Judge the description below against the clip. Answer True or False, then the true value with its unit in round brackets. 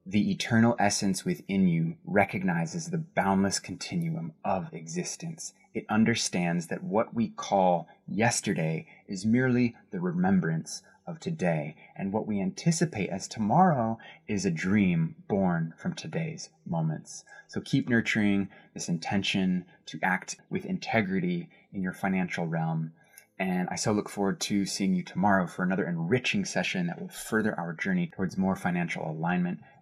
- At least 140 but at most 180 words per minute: True (145 wpm)